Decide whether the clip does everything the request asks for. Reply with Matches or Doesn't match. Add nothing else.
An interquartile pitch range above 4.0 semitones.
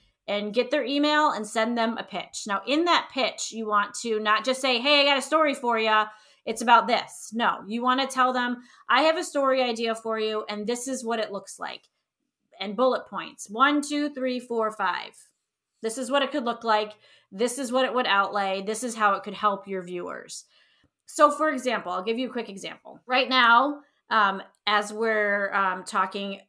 Doesn't match